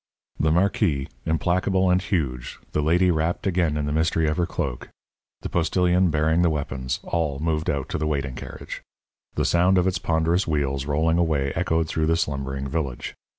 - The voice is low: Yes, very low, 80 Hz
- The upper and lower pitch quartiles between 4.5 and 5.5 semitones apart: No, average, 3.2 semitones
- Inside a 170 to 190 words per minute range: Yes, average, 180 wpm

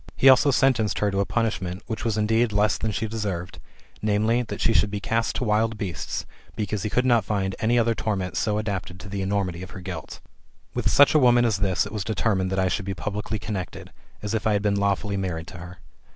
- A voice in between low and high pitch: No, low, 105 Hz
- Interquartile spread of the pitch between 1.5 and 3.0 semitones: Yes, average, 2.7 semitones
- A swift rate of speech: Yes, fast, 235 wpm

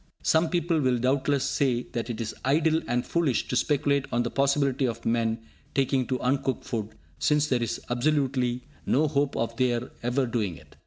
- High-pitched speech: No, low, 130 Hz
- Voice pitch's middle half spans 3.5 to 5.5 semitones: No, average, 2.9 semitones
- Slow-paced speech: No, average, 180 wpm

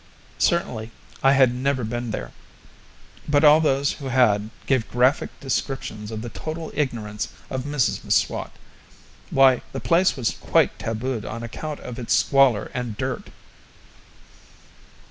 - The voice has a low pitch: Yes, low, 130 Hz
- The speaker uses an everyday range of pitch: Yes, average, 3.7 semitones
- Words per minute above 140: No, slow, 135 wpm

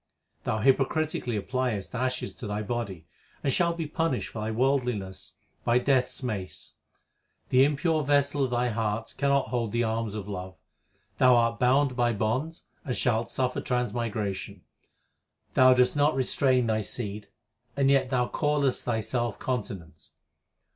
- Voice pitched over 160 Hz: No, low, 125 Hz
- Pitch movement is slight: No, average, 3.6 semitones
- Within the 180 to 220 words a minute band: No, average, 150 wpm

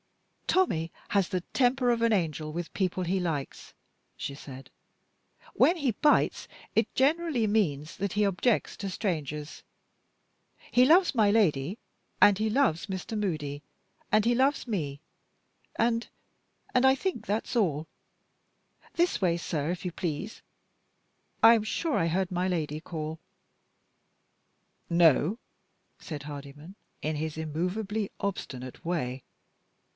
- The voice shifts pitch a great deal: Yes, wide, 6.4 semitones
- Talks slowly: Yes, slow, 130 wpm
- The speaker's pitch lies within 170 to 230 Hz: Yes, medium, 185 Hz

